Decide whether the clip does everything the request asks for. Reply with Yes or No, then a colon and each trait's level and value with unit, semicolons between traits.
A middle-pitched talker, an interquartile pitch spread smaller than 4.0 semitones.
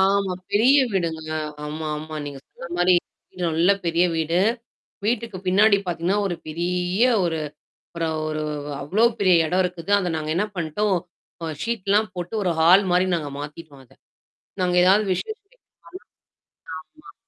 Yes: medium, 180 Hz; average, 3.6 semitones